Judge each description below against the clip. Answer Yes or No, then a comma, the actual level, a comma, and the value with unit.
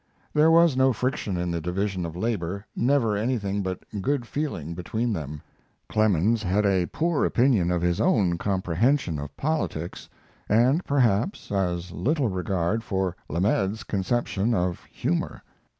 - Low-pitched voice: Yes, low, 100 Hz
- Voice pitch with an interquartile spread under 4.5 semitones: No, wide, 5.6 semitones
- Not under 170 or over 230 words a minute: No, average, 140 wpm